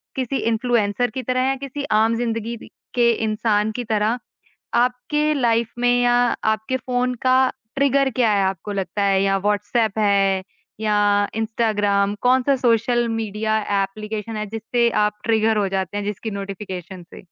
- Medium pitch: No, high, 220 Hz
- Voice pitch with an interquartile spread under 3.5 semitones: Yes, average, 2.9 semitones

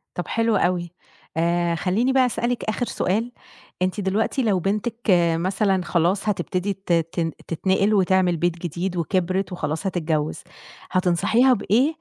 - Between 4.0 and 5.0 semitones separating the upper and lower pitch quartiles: No, average, 3.6 semitones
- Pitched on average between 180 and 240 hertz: Yes, medium, 185 Hz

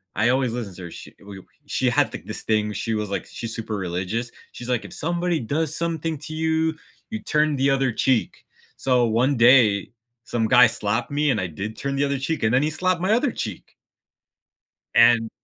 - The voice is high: No, low, 125 Hz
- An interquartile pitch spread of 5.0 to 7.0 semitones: Yes, wide, 5.6 semitones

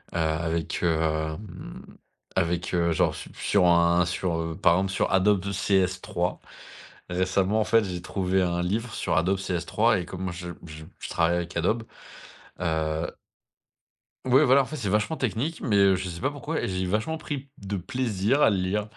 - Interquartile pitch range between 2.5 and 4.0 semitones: Yes, average, 3.6 semitones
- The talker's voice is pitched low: Yes, very low, 95 Hz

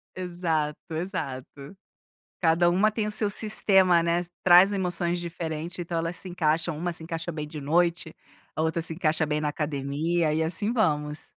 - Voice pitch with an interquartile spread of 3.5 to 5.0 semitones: No, narrow, 2.4 semitones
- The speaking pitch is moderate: Yes, medium, 170 Hz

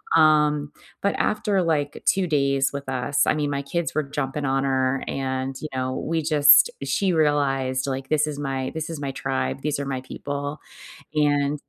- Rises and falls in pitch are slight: Yes, narrow, 2.1 semitones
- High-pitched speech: No, medium, 145 Hz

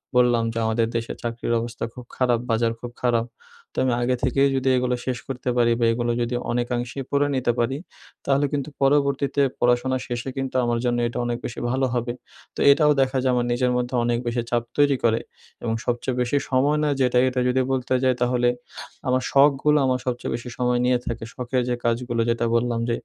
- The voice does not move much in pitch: Yes, narrow, 1.7 semitones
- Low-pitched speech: Yes, low, 125 Hz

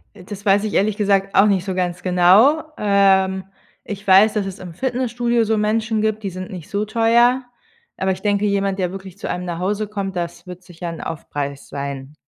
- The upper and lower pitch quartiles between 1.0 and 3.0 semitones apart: Yes, average, 2.7 semitones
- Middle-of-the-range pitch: No, high, 195 Hz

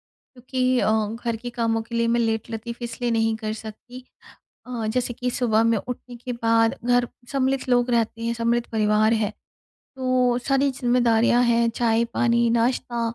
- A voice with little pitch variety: Yes, narrow, 1.4 semitones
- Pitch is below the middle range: No, high, 235 Hz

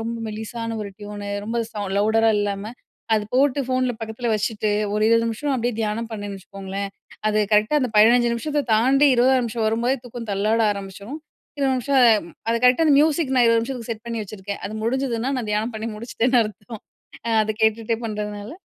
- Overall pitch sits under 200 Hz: No, high, 225 Hz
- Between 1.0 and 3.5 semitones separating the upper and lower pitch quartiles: Yes, average, 2.7 semitones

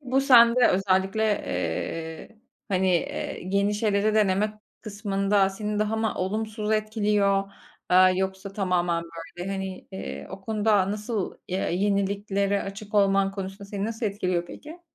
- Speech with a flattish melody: Yes, narrow, 1.9 semitones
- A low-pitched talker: No, high, 200 Hz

